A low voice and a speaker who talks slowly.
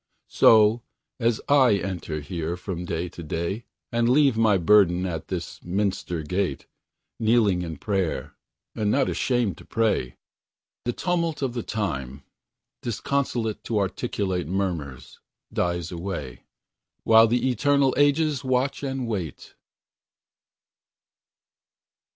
Yes: low, 105 Hz; slow, 115 wpm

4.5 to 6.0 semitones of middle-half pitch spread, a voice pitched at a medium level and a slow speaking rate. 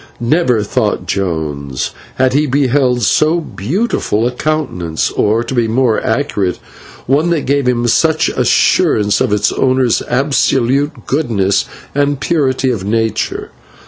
No: average, 5.0 semitones; low, 125 Hz; slow, 130 wpm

